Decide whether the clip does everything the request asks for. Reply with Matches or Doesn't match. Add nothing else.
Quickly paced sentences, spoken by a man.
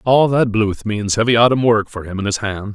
Matches